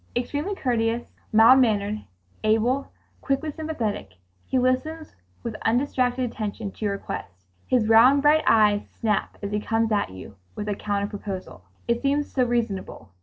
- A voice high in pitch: Yes, high, 225 Hz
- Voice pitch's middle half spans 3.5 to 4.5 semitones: Yes, average, 3.8 semitones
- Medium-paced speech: Yes, average, 150 wpm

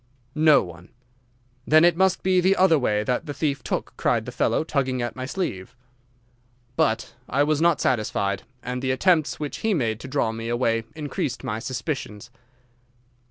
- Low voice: Yes, low, 130 Hz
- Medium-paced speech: Yes, average, 170 wpm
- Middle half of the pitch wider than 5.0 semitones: Yes, wide, 5.6 semitones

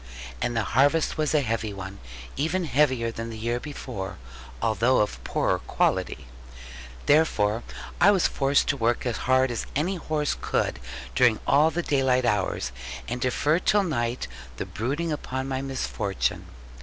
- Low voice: Yes, low, 130 Hz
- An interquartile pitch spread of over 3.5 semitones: Yes, average, 4.5 semitones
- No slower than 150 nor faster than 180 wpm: Yes, average, 155 wpm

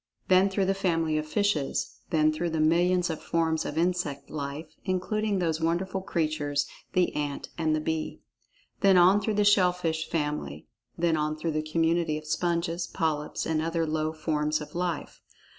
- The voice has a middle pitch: Yes, medium, 165 Hz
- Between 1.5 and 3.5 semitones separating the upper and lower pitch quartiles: Yes, narrow, 2.6 semitones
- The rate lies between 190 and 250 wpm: No, average, 175 wpm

